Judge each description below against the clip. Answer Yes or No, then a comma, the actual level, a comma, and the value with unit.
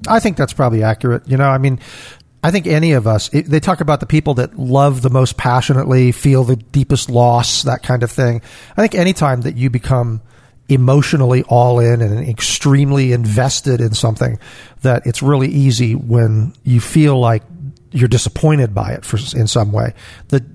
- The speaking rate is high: No, average, 185 wpm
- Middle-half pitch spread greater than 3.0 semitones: No, average, 2.7 semitones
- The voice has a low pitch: Yes, low, 130 Hz